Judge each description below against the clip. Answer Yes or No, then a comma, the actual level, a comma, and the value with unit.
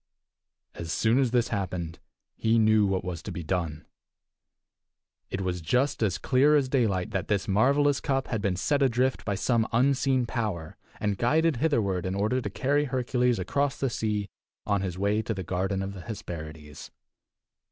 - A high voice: No, low, 110 Hz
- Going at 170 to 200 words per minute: Yes, average, 175 wpm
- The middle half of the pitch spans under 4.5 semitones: No, wide, 5.5 semitones